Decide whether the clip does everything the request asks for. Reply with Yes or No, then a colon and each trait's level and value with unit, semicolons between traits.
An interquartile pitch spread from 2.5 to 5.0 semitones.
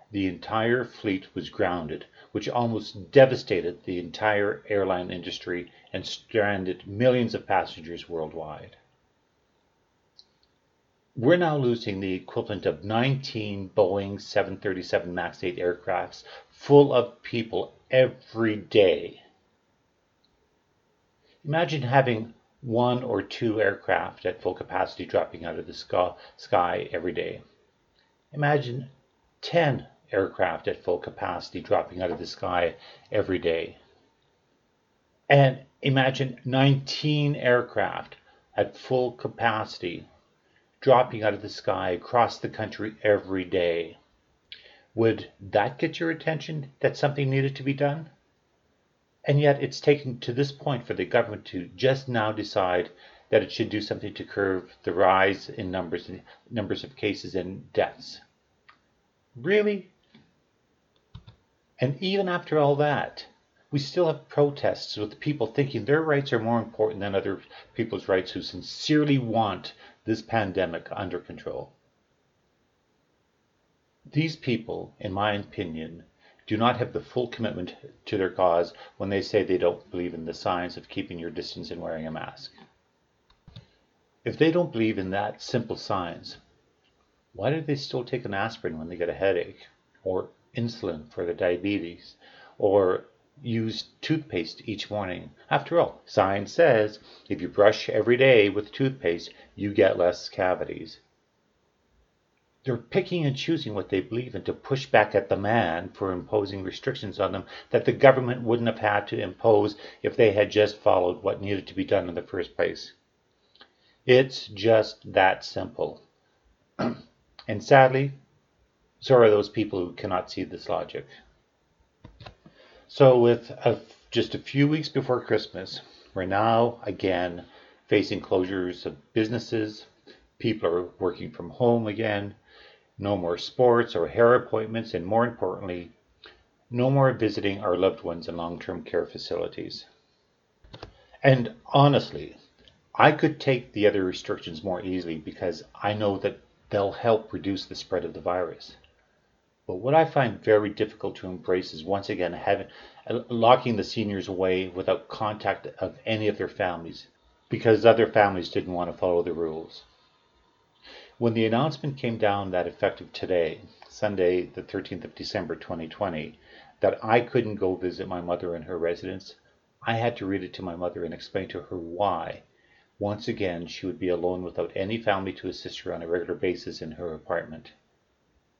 No: wide, 5.5 semitones